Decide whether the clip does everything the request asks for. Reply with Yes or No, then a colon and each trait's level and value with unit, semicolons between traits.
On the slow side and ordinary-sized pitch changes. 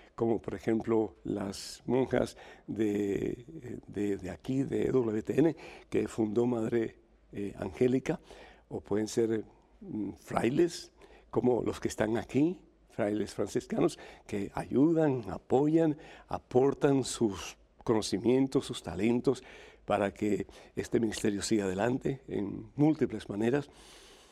Yes: slow, 110 wpm; average, 4.0 semitones